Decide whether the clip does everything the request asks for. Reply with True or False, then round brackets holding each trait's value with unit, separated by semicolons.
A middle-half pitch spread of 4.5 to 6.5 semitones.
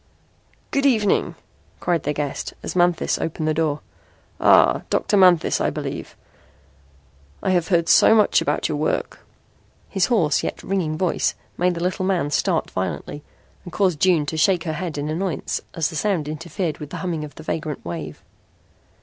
False (3.4 semitones)